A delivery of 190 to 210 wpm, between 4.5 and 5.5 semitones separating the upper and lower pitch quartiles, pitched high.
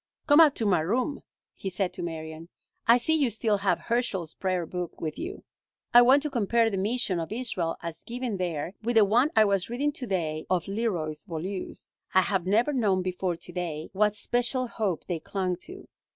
Yes: average, 200 wpm; average, 5.2 semitones; high, 200 Hz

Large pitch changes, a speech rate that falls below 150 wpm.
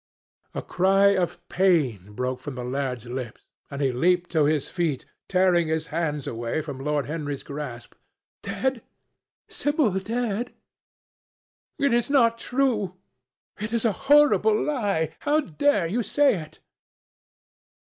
Yes: wide, 7.8 semitones; slow, 135 wpm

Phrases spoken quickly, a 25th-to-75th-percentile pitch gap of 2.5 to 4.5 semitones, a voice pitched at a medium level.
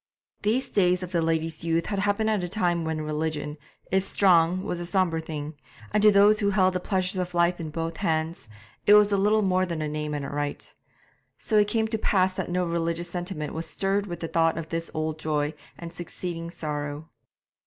Yes: fast, 210 wpm; average, 3.1 semitones; medium, 170 Hz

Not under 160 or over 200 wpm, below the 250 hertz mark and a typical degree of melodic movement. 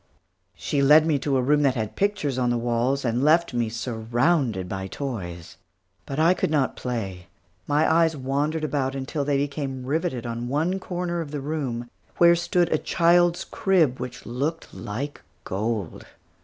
Yes: average, 170 wpm; medium, 140 Hz; average, 4.8 semitones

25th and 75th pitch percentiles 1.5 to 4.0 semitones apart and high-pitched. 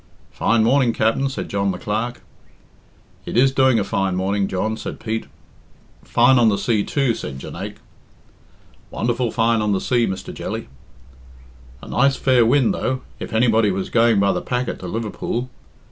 No: average, 3.5 semitones; low, 115 Hz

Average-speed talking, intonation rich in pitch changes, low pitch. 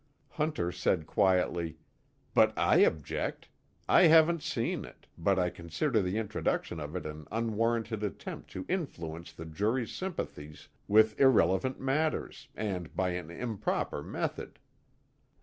No: slow, 130 wpm; wide, 6.1 semitones; very low, 95 Hz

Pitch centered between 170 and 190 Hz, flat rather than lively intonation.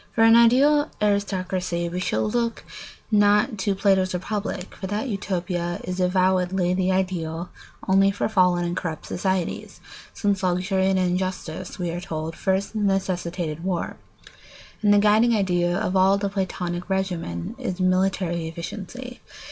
Yes: medium, 185 Hz; narrow, 2.2 semitones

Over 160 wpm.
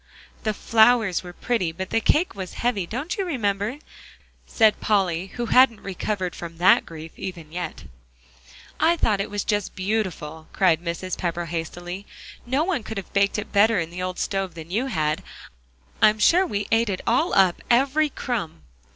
Yes: average, 170 wpm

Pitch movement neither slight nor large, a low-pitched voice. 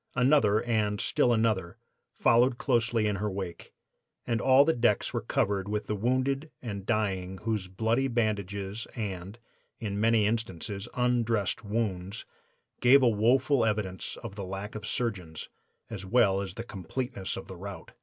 Yes: average, 3.3 semitones; low, 110 Hz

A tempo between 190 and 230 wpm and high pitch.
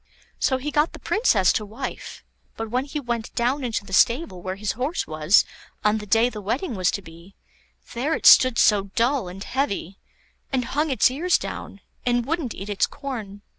Yes: average, 195 wpm; high, 235 Hz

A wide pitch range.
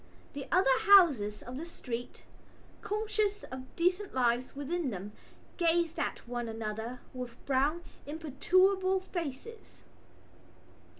Yes: wide, 6.9 semitones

